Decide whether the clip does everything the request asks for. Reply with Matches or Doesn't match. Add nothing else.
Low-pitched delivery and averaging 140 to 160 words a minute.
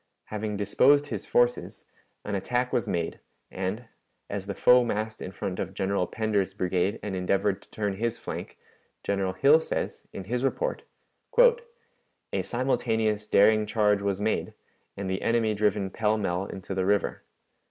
Matches